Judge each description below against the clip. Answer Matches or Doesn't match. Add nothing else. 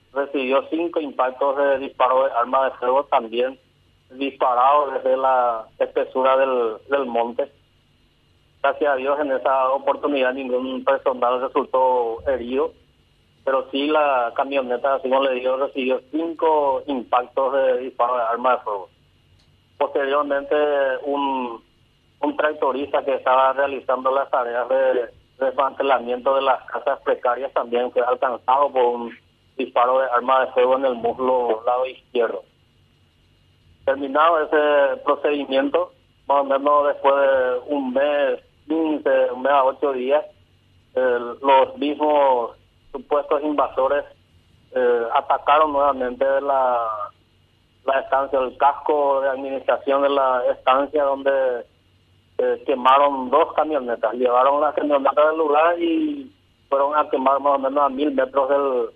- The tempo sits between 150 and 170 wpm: Doesn't match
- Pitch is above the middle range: Doesn't match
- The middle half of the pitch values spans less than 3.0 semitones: Matches